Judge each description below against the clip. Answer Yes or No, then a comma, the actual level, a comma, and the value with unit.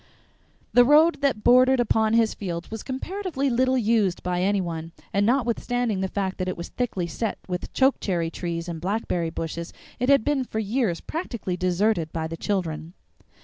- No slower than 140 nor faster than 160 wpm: No, average, 175 wpm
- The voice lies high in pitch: Yes, high, 205 Hz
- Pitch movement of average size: No, wide, 5.9 semitones